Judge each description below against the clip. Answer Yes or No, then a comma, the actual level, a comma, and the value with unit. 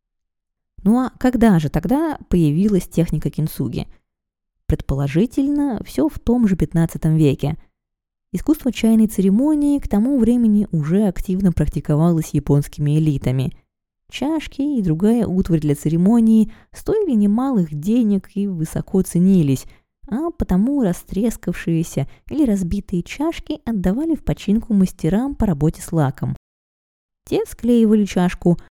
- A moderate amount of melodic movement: No, wide, 6.5 semitones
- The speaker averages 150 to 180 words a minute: No, average, 115 wpm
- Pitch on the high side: Yes, high, 195 Hz